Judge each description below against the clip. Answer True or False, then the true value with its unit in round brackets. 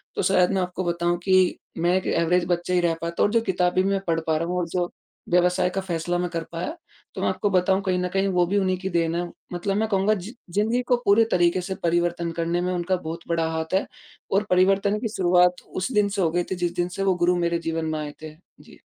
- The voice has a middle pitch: True (180 Hz)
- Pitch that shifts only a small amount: True (1.9 semitones)